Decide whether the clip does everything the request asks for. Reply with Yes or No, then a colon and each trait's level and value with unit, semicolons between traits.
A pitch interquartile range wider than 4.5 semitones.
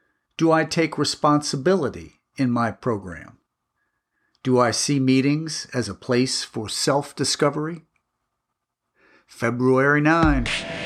No: average, 3.6 semitones